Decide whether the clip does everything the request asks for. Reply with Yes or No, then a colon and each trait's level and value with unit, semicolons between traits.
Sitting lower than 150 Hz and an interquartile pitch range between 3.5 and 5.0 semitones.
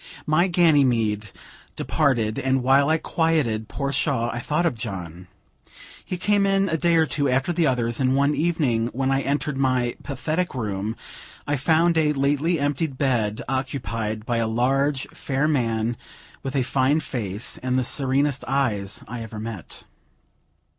Yes: low, 135 Hz; average, 4.4 semitones